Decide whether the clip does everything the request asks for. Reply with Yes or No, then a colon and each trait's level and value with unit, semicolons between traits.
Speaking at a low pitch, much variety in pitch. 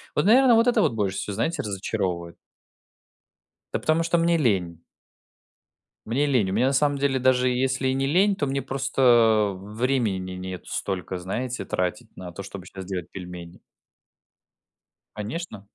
Yes: low, 120 Hz; wide, 6.3 semitones